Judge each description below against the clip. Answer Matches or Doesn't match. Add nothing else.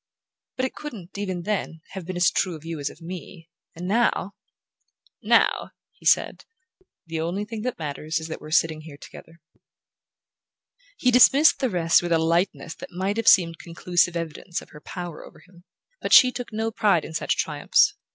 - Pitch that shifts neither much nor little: Matches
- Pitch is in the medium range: Matches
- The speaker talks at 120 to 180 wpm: Doesn't match